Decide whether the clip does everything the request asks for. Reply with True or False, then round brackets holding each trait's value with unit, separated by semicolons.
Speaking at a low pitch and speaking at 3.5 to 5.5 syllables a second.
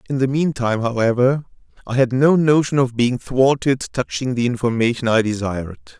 True (125 Hz; 5.4 syllables/s)